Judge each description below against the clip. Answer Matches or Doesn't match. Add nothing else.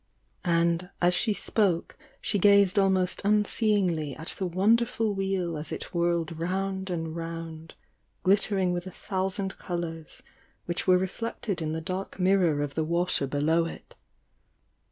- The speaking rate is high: Doesn't match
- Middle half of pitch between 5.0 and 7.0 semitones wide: Doesn't match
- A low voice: Doesn't match